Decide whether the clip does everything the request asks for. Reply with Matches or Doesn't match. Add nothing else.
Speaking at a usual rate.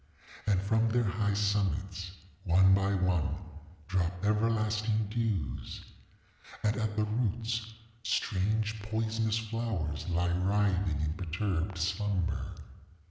Doesn't match